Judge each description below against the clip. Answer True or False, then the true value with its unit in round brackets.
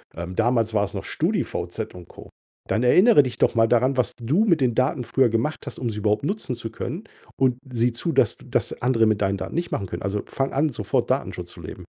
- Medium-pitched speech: False (120 Hz)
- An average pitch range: True (3.6 semitones)